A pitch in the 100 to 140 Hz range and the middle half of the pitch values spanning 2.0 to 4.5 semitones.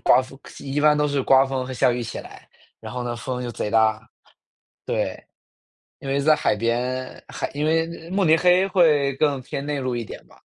Yes: low, 135 Hz; average, 3.3 semitones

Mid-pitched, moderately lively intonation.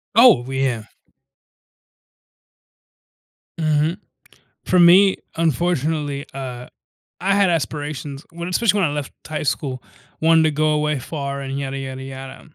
Yes: medium, 150 Hz; average, 3.7 semitones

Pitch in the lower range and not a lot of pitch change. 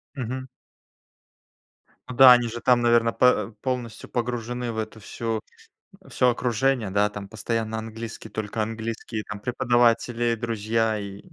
Yes: low, 115 Hz; narrow, 1.9 semitones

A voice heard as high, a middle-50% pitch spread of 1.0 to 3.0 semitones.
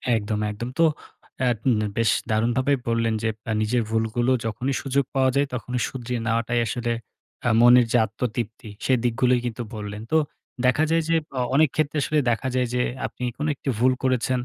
No: low, 120 Hz; narrow, 2.4 semitones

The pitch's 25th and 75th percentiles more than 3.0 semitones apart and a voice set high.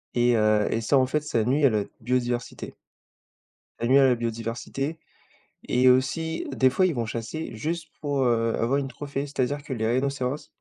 No: average, 3.4 semitones; low, 130 Hz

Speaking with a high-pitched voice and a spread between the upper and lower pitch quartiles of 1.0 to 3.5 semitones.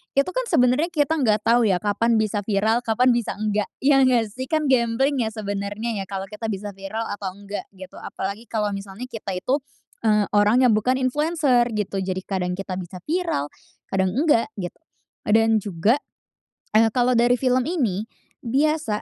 No: high, 220 Hz; average, 4.1 semitones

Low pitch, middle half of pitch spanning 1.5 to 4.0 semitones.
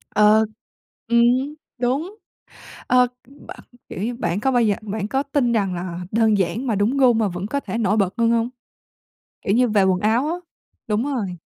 No: high, 220 Hz; average, 3.7 semitones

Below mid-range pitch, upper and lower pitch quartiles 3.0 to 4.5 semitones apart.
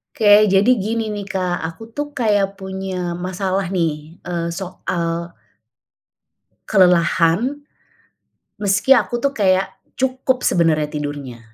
No: high, 195 Hz; average, 3.7 semitones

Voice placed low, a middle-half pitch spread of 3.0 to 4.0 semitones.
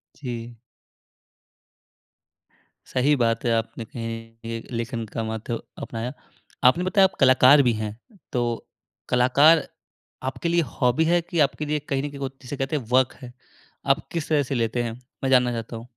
Yes: low, 125 Hz; average, 3.7 semitones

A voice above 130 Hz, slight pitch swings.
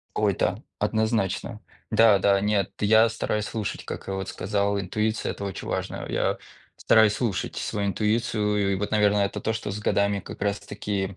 No: low, 105 Hz; narrow, 1.6 semitones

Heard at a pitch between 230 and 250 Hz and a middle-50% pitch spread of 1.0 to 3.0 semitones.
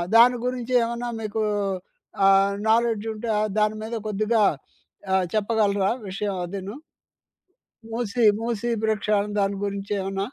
No: high, 215 Hz; narrow, 2.5 semitones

